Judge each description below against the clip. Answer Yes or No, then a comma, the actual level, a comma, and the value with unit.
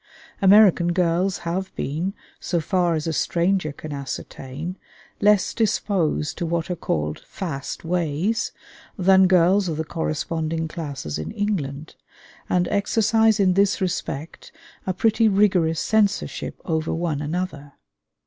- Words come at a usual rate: No, slow, 130 wpm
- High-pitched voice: No, medium, 175 Hz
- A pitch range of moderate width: Yes, average, 3.7 semitones